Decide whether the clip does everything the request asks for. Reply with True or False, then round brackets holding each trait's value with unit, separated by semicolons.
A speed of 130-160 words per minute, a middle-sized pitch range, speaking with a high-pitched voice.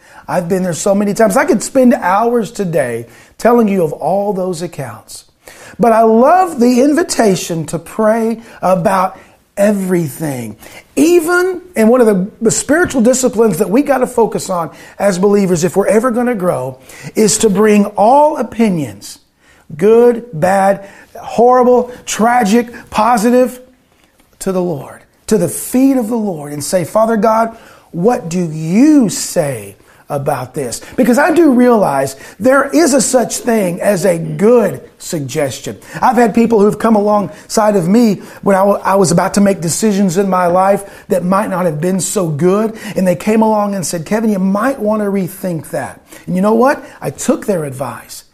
False (170 wpm; 4.7 semitones; 205 Hz)